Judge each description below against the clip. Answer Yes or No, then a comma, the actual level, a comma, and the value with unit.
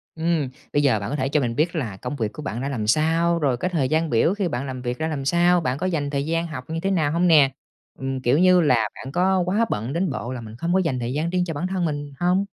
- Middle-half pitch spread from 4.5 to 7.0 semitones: Yes, average, 4.9 semitones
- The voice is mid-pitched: Yes, medium, 150 Hz